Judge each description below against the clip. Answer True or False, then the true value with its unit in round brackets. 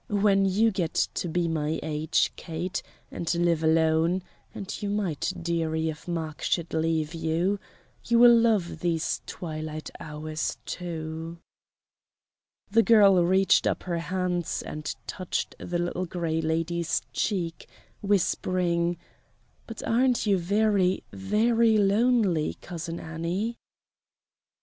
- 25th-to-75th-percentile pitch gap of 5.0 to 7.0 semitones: False (3.4 semitones)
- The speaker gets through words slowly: True (120 wpm)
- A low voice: False (175 Hz)